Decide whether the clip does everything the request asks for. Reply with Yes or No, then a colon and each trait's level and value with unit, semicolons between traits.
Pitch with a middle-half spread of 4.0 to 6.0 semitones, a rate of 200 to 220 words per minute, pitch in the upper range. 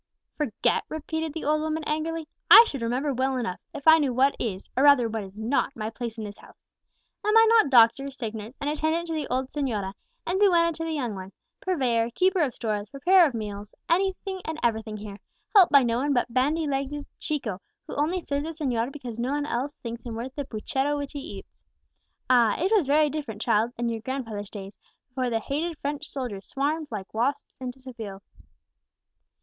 Yes: average, 5.1 semitones; fast, 205 wpm; very high, 270 Hz